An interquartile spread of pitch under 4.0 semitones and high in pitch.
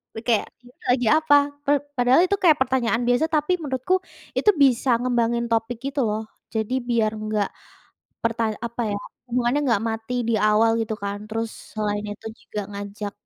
Yes: average, 2.9 semitones; high, 235 Hz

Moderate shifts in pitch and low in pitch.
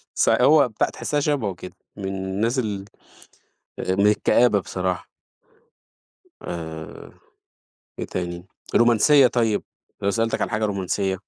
Yes: average, 4.0 semitones; low, 100 Hz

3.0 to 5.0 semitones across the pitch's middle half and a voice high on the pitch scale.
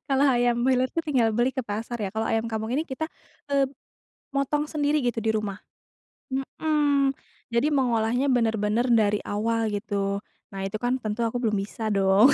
Yes: average, 3.7 semitones; high, 235 Hz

